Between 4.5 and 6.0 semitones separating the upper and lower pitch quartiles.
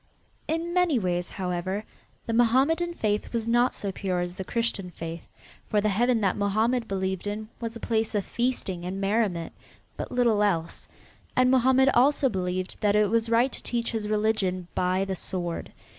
No: average, 4.1 semitones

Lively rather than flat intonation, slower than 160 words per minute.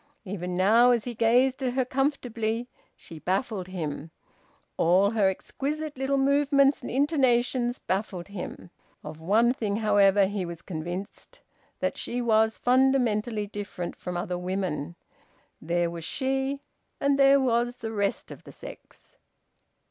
Yes: wide, 5.9 semitones; average, 140 wpm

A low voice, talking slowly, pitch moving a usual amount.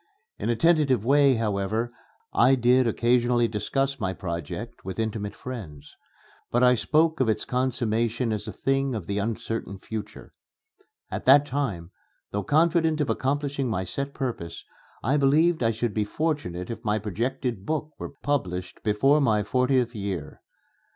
No: low, 120 Hz; average, 150 wpm; average, 4.6 semitones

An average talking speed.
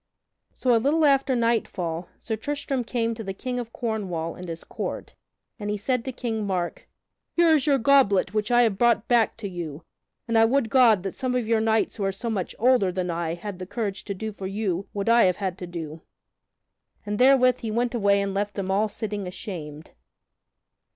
No: fast, 210 wpm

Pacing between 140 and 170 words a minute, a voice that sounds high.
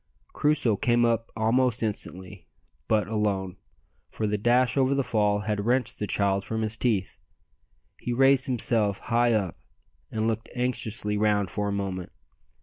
No: average, 150 wpm; low, 110 Hz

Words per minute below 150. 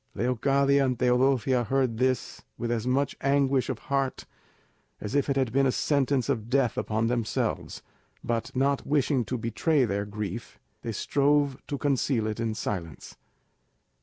No: average, 155 wpm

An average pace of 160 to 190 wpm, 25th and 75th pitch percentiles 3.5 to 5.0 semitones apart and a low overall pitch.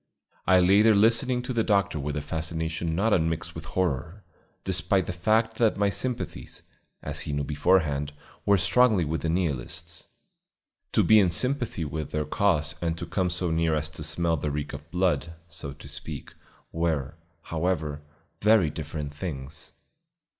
Yes: average, 165 wpm; average, 4.5 semitones; very low, 85 Hz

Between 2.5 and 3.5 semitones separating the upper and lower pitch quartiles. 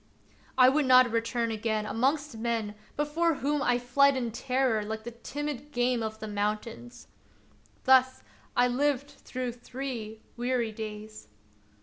Yes: average, 3.2 semitones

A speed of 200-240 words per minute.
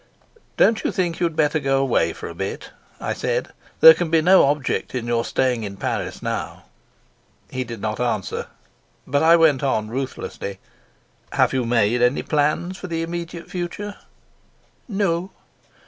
No: average, 160 wpm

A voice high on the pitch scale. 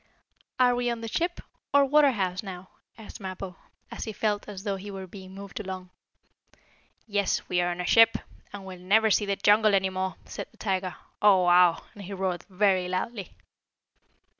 Yes: high, 195 Hz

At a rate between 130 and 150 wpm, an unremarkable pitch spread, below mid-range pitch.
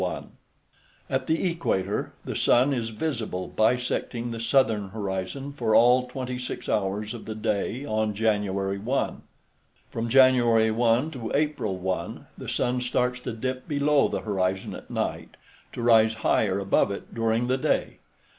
Yes: average, 145 wpm; average, 3.2 semitones; low, 115 Hz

